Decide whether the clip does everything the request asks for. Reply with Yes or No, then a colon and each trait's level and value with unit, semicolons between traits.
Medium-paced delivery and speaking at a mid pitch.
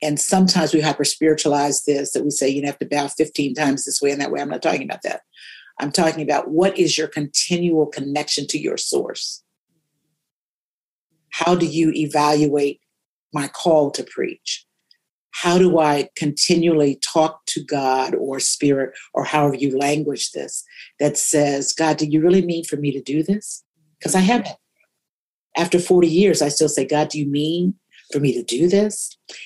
Yes: average, 175 wpm; medium, 155 Hz